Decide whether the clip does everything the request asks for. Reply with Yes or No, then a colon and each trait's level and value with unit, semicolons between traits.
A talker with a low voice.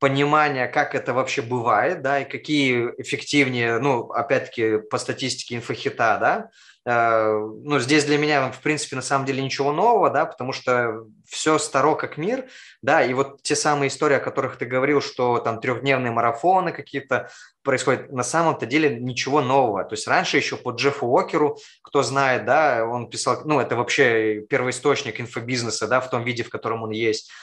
Yes: low, 130 Hz